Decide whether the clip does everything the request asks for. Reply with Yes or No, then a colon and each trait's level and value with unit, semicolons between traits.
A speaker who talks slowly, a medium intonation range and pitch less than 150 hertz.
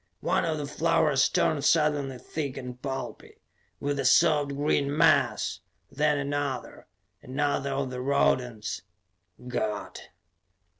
No: slow, 115 wpm; narrow, 2.3 semitones; medium, 140 Hz